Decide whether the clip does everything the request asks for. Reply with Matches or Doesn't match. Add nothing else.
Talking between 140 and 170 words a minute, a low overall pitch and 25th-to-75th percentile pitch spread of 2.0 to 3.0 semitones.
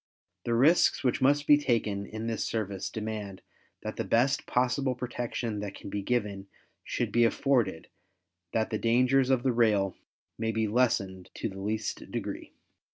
Doesn't match